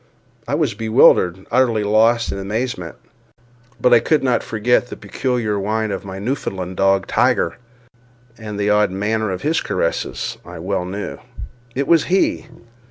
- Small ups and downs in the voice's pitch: No, average, 3.9 semitones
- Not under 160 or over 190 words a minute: No, average, 150 wpm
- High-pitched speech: No, low, 110 Hz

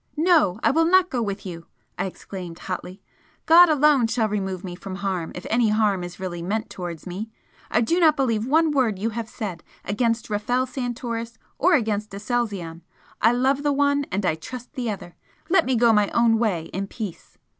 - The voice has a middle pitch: No, high, 220 Hz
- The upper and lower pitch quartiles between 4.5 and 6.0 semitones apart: Yes, average, 5.0 semitones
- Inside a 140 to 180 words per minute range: No, average, 195 wpm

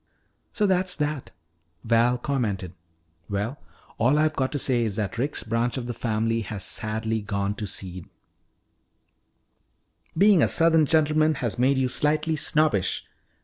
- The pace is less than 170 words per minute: Yes, average, 145 wpm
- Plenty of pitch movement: Yes, wide, 5.9 semitones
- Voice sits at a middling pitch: No, low, 120 Hz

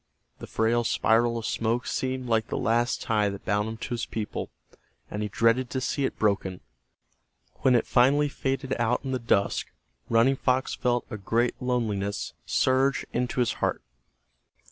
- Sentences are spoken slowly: No, average, 165 wpm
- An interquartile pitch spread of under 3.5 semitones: Yes, narrow, 2.6 semitones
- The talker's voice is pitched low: Yes, low, 120 Hz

